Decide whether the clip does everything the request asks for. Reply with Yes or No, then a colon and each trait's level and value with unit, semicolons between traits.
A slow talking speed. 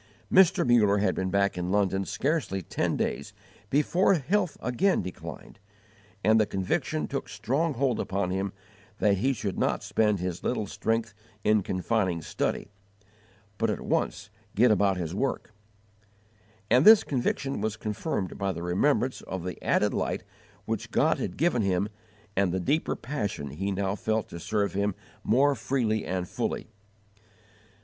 No: average, 155 wpm